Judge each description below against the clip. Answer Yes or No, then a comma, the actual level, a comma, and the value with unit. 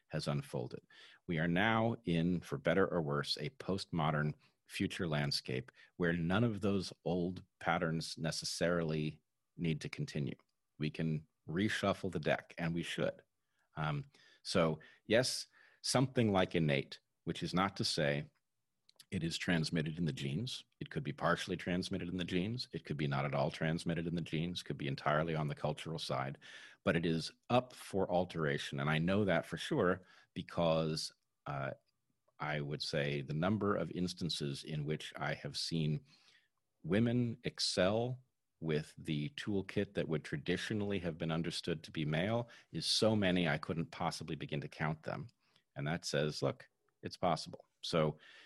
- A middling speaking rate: Yes, average, 165 wpm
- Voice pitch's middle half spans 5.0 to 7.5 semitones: No, average, 3.4 semitones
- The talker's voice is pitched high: No, very low, 85 Hz